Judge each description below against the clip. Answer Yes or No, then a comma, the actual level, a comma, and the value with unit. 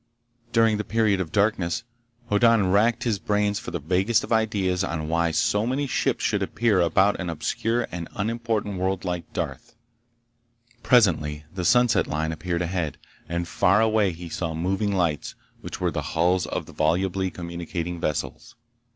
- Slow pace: No, average, 160 wpm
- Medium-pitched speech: No, very low, 95 Hz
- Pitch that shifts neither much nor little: Yes, average, 4.2 semitones